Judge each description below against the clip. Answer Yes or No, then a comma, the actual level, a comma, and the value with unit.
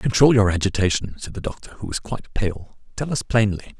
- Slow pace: No, fast, 205 wpm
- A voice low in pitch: Yes, low, 105 Hz